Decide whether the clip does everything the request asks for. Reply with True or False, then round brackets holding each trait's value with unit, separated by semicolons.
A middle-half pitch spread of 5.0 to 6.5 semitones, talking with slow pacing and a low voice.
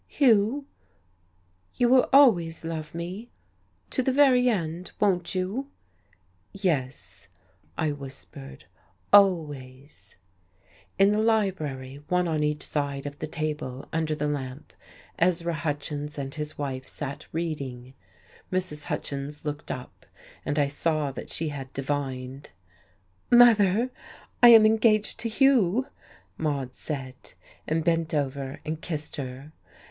False (5.6 semitones; 120 wpm; 155 Hz)